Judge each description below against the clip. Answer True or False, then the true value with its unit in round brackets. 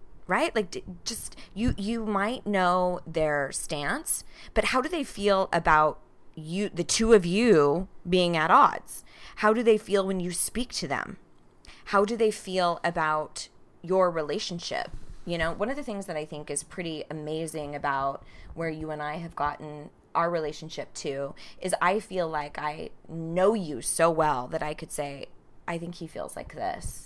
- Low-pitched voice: False (170 Hz)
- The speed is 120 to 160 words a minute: False (175 wpm)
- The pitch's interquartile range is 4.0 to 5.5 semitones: True (4.5 semitones)